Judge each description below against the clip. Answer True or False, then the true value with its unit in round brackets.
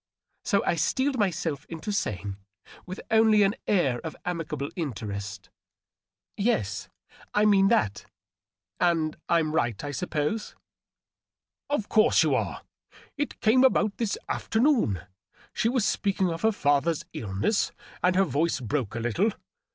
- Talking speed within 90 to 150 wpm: True (145 wpm)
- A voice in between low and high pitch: True (170 Hz)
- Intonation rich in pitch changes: True (8.1 semitones)